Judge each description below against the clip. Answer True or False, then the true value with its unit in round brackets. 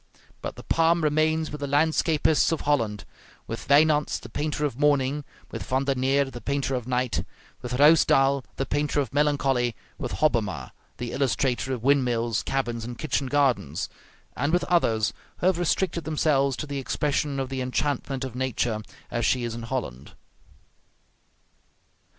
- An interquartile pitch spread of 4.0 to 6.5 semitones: False (3.3 semitones)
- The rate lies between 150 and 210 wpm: True (160 wpm)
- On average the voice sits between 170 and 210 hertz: False (135 Hz)